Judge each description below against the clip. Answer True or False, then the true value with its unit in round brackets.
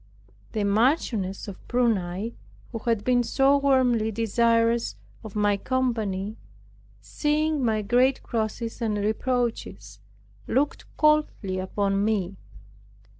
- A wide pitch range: False (3.7 semitones)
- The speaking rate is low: True (105 wpm)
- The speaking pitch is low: False (225 Hz)